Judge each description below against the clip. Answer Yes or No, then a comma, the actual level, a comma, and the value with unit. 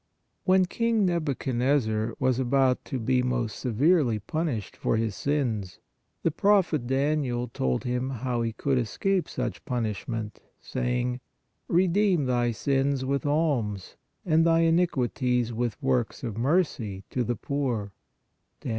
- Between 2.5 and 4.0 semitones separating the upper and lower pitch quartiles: No, average, 4.4 semitones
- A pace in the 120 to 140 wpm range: Yes, slow, 135 wpm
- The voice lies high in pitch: No, low, 130 Hz